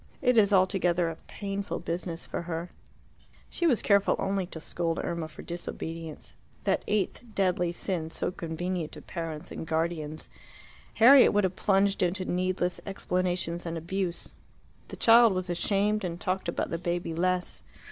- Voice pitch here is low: No, medium, 180 Hz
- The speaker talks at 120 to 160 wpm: Yes, average, 155 wpm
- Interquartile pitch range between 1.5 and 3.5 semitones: Yes, narrow, 2.6 semitones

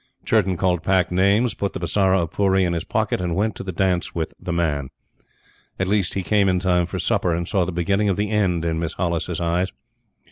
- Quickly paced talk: Yes, fast, 225 wpm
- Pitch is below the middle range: Yes, very low, 90 Hz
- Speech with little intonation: Yes, narrow, 2.3 semitones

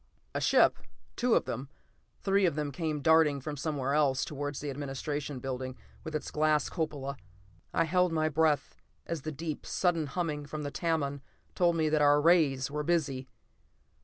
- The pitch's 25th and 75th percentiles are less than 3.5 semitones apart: Yes, narrow, 2.4 semitones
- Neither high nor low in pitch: Yes, medium, 150 Hz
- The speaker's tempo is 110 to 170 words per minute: Yes, average, 165 wpm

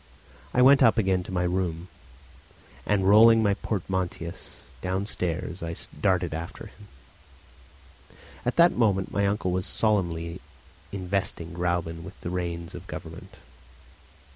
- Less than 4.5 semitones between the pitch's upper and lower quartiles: Yes, average, 2.9 semitones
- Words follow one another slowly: Yes, slow, 125 wpm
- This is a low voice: Yes, very low, 95 Hz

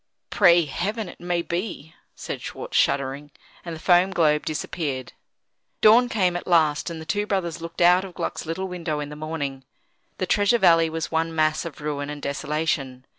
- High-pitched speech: No, medium, 165 Hz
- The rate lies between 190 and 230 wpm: No, average, 180 wpm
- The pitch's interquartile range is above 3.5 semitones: No, average, 3.1 semitones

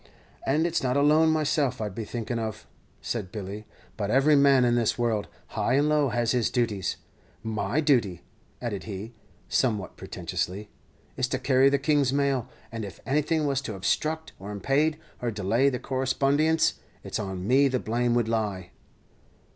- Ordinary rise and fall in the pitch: Yes, average, 4.5 semitones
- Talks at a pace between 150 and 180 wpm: Yes, average, 165 wpm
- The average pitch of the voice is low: Yes, low, 125 Hz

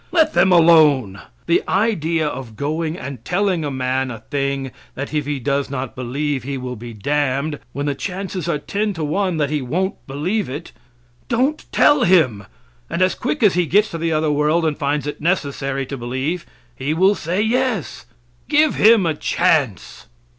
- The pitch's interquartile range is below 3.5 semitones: No, average, 5.0 semitones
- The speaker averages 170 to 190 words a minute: Yes, average, 180 wpm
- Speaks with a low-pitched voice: No, medium, 150 Hz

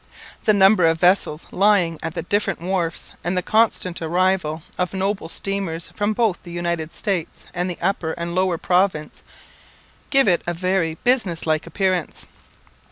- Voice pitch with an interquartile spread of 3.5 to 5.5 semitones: No, average, 2.7 semitones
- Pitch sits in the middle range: Yes, medium, 180 Hz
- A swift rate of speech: No, average, 160 wpm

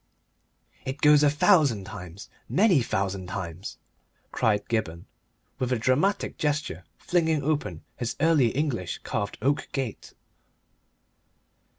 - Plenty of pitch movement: Yes, wide, 6.8 semitones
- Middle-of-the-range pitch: No, low, 130 Hz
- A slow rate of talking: Yes, slow, 110 wpm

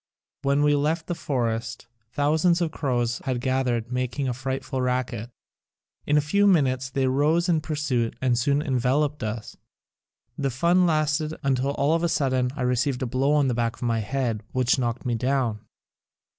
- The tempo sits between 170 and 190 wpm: Yes, average, 175 wpm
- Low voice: Yes, low, 130 Hz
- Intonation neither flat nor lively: Yes, average, 3.2 semitones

